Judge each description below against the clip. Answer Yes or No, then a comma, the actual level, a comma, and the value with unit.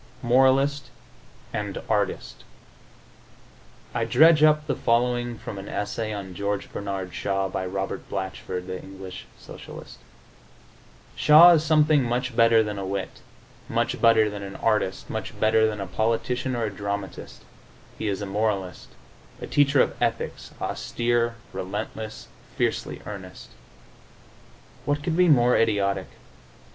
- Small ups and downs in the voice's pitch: No, average, 4.1 semitones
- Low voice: Yes, low, 110 Hz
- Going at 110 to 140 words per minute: Yes, slow, 135 wpm